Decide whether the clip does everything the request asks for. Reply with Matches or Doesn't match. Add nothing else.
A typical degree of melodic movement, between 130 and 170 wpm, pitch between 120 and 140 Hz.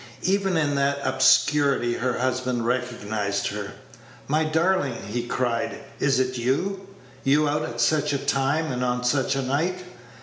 Matches